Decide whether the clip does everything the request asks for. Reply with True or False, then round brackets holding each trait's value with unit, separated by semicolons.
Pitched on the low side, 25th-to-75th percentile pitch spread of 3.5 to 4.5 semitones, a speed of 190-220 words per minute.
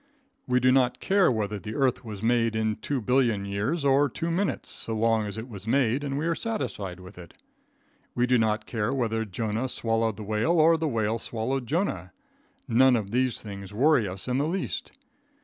True (115 Hz; 4.0 semitones; 200 wpm)